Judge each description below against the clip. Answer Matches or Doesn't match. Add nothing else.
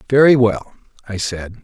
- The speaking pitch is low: Matches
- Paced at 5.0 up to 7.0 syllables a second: Doesn't match